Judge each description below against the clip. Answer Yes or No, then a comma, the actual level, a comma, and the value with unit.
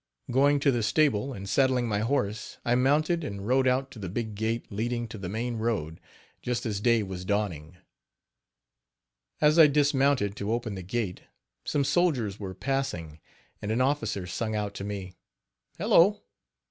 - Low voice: Yes, low, 115 Hz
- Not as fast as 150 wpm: No, average, 165 wpm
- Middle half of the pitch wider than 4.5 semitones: Yes, average, 5.0 semitones